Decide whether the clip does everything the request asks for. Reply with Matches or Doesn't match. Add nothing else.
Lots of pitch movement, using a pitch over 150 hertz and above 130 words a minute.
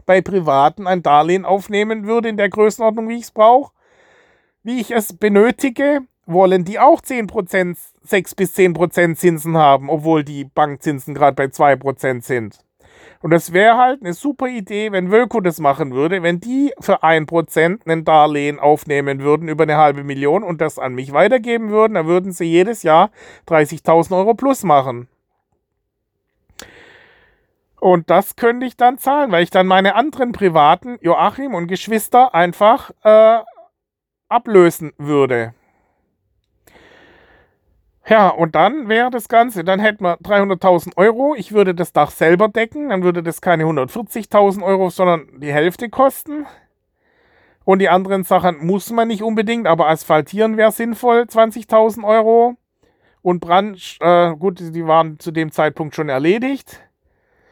Matches